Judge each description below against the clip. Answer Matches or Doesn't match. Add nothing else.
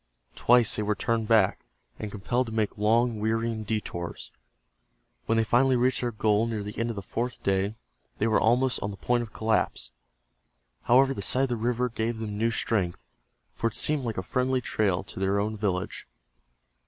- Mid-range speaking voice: Doesn't match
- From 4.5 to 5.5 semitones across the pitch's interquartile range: Doesn't match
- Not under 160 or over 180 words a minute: Doesn't match